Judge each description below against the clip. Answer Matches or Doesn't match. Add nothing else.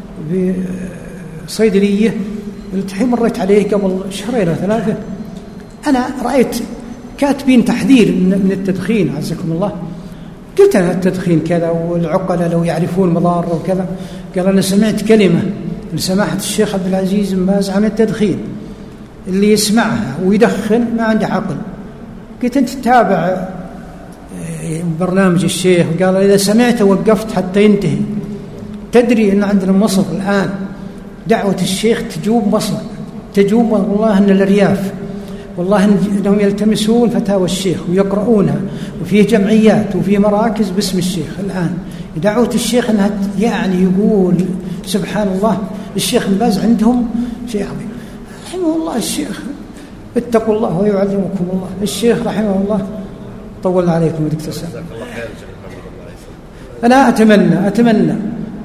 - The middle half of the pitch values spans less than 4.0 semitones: Matches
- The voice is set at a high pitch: Matches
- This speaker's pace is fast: Doesn't match